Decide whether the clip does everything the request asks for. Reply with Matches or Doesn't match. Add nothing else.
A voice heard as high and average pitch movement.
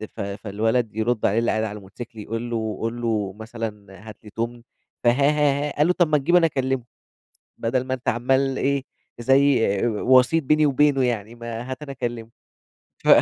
Doesn't match